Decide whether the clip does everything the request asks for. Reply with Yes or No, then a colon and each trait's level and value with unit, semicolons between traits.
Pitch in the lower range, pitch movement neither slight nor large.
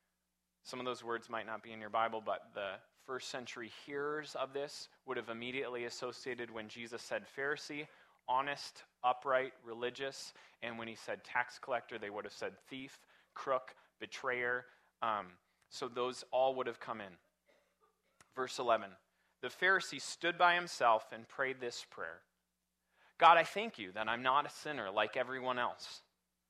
Yes: low, 125 Hz; average, 3.4 semitones